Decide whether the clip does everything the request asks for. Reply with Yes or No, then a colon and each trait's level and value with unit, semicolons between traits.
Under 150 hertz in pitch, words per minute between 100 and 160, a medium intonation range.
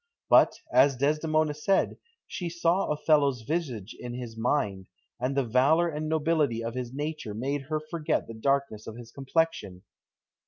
Yes: medium, 140 Hz; average, 155 wpm; average, 4.7 semitones